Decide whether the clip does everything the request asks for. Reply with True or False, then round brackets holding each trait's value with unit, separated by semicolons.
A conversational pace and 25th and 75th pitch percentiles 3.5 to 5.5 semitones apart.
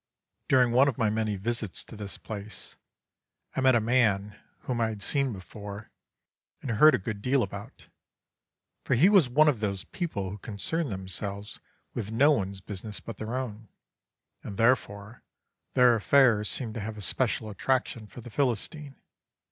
True (165 wpm; 4.0 semitones)